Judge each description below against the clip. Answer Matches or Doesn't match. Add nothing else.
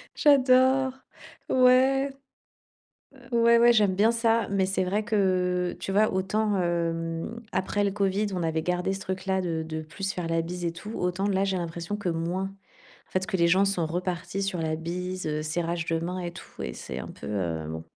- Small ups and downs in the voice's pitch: Doesn't match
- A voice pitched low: Doesn't match